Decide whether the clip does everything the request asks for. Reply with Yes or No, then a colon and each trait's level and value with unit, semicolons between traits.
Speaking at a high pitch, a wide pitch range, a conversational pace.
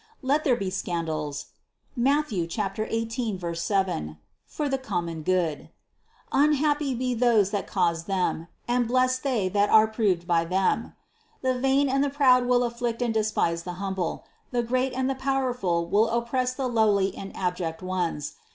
Yes: high, 220 Hz; wide, 5.9 semitones; average, 160 wpm